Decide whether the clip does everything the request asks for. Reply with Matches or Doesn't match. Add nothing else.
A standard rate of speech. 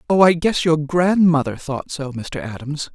Matches